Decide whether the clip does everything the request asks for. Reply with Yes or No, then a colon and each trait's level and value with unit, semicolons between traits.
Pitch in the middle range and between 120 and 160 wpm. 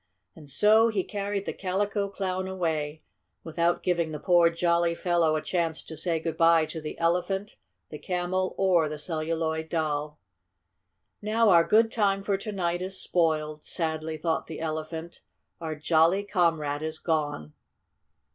Yes: medium, 170 Hz; average, 155 wpm